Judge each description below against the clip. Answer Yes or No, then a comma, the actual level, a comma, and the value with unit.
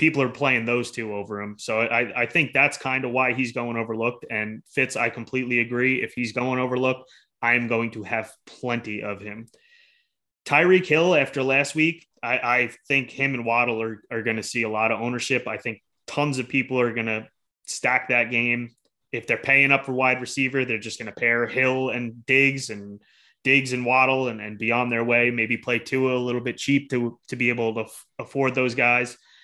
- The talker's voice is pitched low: Yes, low, 120 Hz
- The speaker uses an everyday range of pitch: No, narrow, 2.2 semitones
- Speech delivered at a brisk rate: Yes, fast, 215 wpm